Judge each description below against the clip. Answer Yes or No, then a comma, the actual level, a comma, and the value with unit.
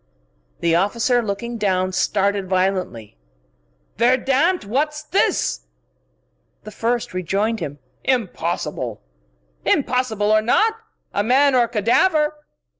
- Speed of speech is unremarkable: No, slow, 110 wpm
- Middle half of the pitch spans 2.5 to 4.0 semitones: No, average, 5.3 semitones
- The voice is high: Yes, high, 220 Hz